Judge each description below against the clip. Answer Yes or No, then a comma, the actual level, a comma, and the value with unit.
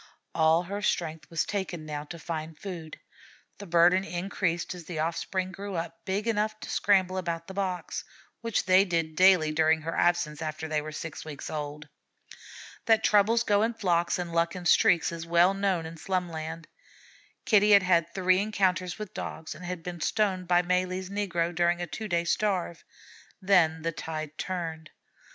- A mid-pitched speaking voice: Yes, medium, 175 Hz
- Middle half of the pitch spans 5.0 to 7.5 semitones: No, average, 2.8 semitones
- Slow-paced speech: No, average, 175 wpm